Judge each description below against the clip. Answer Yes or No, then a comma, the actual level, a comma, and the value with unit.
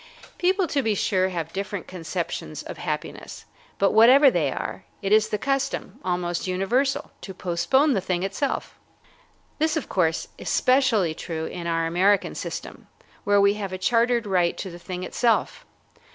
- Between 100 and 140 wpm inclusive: No, average, 165 wpm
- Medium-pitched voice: No, high, 195 Hz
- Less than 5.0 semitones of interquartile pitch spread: No, average, 5.3 semitones